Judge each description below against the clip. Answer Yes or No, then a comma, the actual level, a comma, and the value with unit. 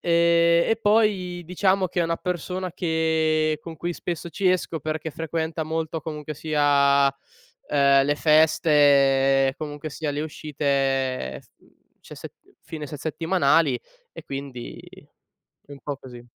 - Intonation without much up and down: No, average, 3.1 semitones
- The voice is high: No, medium, 155 Hz